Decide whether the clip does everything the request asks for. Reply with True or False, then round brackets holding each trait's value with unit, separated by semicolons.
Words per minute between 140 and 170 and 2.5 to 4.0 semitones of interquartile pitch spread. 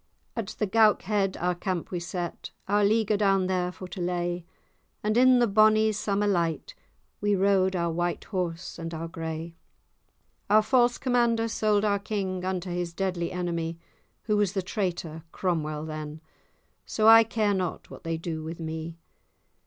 True (160 wpm; 3.7 semitones)